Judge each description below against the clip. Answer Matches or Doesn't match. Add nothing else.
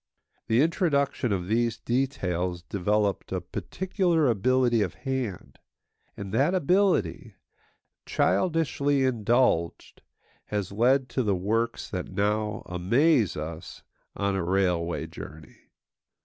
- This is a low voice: Matches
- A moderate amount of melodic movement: Doesn't match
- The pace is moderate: Doesn't match